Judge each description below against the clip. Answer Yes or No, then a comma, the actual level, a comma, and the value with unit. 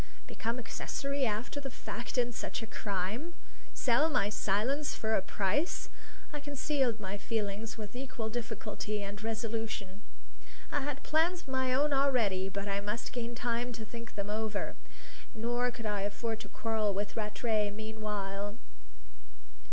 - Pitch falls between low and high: No, high, 225 Hz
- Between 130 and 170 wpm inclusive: Yes, average, 150 wpm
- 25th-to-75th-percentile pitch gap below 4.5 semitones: Yes, average, 3.3 semitones